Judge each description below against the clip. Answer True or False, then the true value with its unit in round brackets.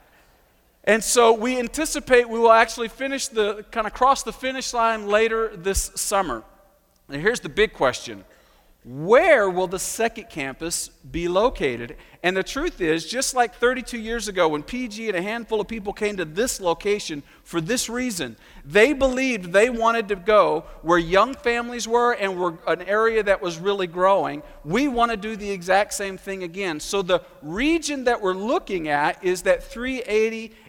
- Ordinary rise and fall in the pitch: True (4.3 semitones)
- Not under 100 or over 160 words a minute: False (175 wpm)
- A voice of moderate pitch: False (215 Hz)